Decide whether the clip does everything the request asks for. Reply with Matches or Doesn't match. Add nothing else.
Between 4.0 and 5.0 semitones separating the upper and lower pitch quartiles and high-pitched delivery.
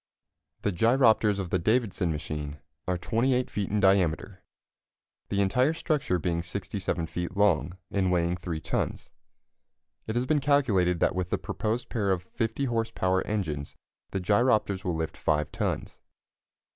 Doesn't match